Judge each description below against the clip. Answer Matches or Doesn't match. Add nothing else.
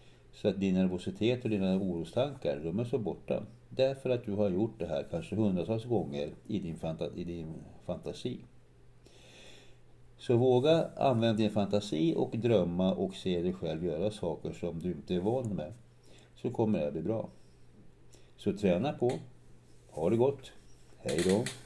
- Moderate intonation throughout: Doesn't match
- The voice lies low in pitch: Matches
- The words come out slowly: Doesn't match